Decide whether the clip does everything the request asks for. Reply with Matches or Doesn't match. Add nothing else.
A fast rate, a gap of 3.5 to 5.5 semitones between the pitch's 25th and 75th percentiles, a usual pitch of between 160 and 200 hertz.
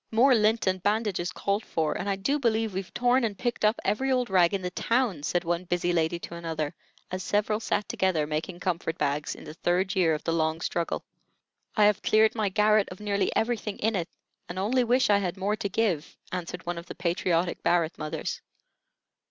Matches